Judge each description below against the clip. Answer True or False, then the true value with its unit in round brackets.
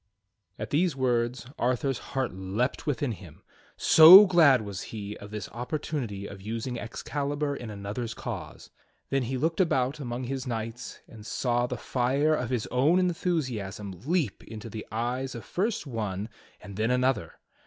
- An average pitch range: True (4.6 semitones)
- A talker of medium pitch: False (125 Hz)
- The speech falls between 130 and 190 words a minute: True (155 wpm)